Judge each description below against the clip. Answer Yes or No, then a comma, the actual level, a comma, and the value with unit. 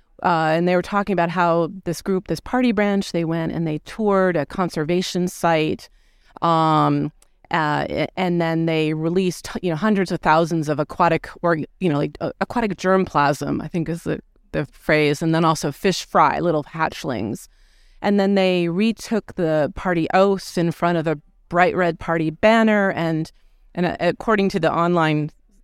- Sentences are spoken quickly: No, average, 175 wpm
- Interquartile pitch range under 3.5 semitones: Yes, average, 2.9 semitones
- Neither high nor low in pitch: Yes, medium, 170 Hz